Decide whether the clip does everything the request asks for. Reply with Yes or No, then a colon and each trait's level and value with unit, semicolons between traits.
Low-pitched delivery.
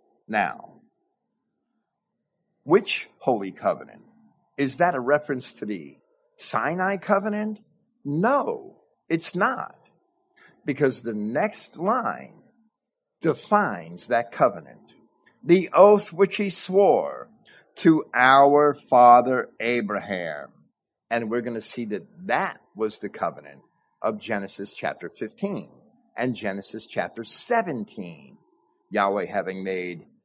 No: medium, 145 Hz